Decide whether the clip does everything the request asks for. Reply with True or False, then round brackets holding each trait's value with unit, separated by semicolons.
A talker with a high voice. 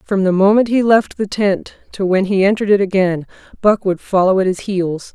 True (195 Hz)